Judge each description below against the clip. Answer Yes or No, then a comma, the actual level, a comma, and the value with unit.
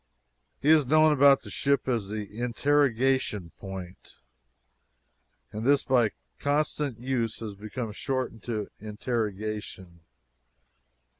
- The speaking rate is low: Yes, slow, 105 wpm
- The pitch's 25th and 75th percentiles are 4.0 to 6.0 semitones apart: Yes, average, 4.5 semitones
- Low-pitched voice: Yes, low, 120 Hz